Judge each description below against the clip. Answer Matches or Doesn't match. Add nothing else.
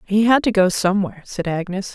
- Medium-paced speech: Doesn't match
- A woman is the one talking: Matches